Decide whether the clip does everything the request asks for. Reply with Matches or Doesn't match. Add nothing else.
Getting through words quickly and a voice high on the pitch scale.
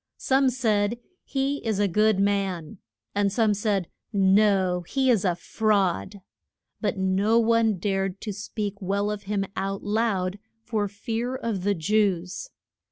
Doesn't match